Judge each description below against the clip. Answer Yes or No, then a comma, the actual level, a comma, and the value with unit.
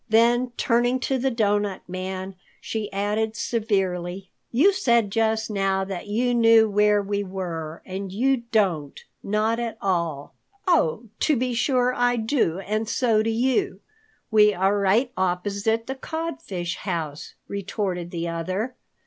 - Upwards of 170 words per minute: No, average, 140 wpm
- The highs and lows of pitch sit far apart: No, average, 3.9 semitones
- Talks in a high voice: Yes, high, 210 Hz